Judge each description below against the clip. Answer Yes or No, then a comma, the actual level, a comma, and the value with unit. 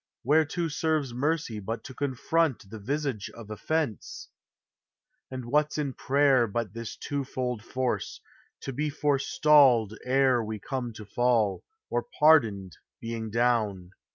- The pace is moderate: No, slow, 130 wpm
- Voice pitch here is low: Yes, low, 125 Hz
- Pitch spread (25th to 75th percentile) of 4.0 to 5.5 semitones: Yes, average, 4.5 semitones